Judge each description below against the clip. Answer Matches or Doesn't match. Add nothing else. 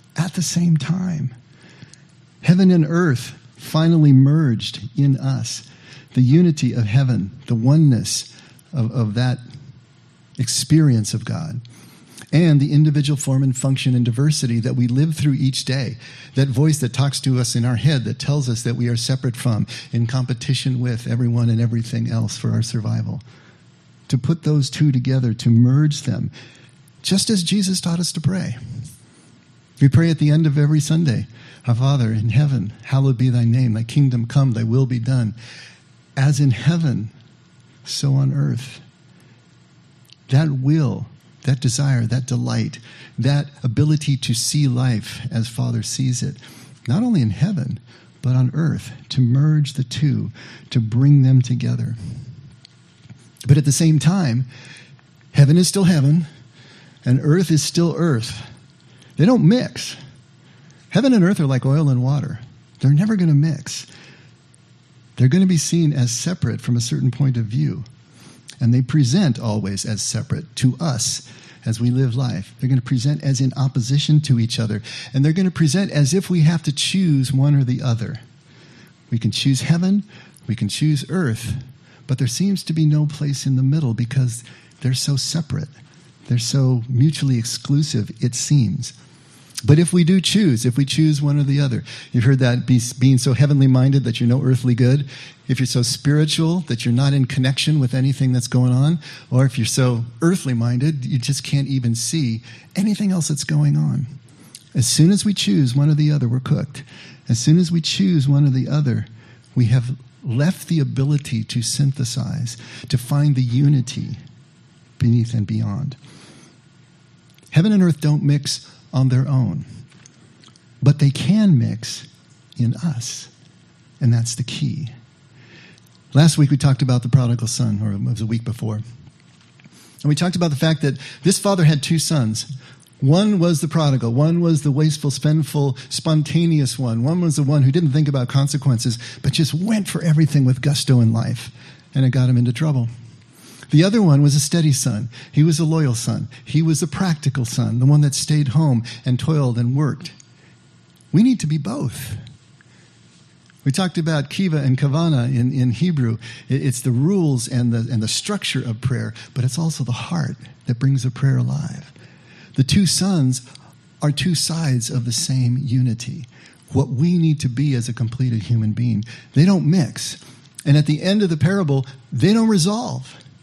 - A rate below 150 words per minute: Doesn't match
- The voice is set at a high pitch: Doesn't match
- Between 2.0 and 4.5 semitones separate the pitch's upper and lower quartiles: Matches